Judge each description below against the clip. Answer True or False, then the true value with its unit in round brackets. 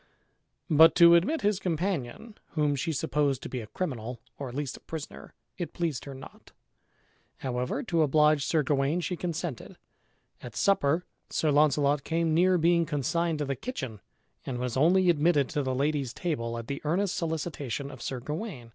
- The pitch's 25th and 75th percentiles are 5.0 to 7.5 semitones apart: False (4.1 semitones)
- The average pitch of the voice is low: False (150 Hz)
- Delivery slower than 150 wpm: False (175 wpm)